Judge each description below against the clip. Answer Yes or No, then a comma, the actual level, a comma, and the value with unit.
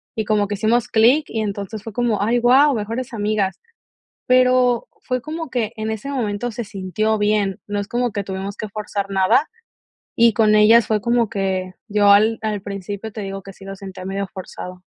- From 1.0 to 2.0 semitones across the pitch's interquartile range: No, average, 2.9 semitones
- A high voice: Yes, high, 215 Hz